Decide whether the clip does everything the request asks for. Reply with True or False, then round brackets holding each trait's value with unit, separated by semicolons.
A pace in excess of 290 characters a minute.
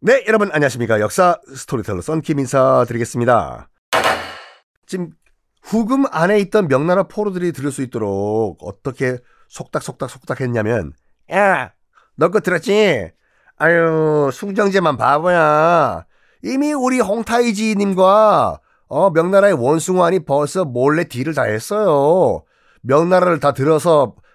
False (275 characters per minute)